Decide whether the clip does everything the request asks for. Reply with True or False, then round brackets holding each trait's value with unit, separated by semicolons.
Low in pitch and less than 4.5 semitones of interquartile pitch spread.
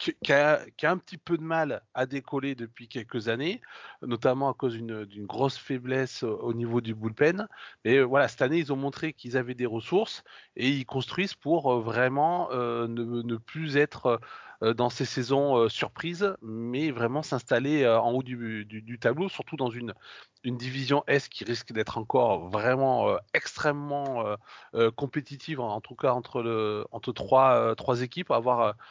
True (130 Hz; 3.7 semitones)